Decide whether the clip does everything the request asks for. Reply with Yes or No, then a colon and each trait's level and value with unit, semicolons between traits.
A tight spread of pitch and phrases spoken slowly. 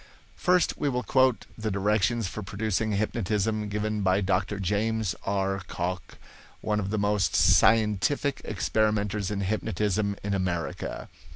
Yes: narrow, 2.0 semitones; slow, 130 wpm